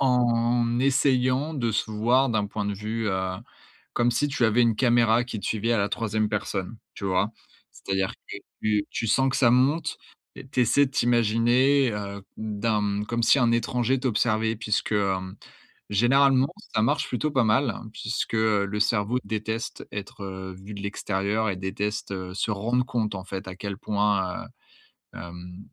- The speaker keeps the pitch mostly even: No, average, 3.1 semitones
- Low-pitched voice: Yes, low, 110 Hz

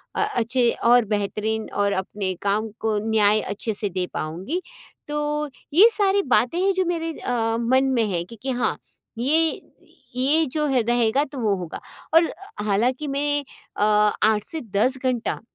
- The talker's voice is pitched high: Yes, high, 235 Hz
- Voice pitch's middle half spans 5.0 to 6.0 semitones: Yes, wide, 5.5 semitones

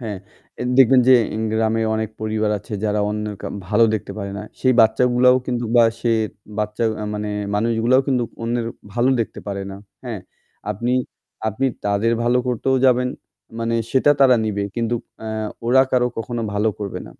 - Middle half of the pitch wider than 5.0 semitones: No, narrow, 2.6 semitones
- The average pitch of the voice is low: Yes, low, 115 Hz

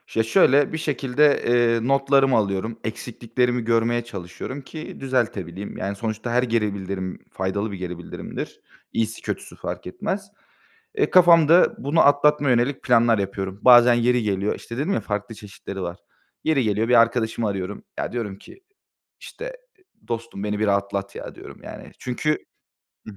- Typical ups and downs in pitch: Yes, average, 4.6 semitones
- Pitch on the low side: Yes, low, 115 Hz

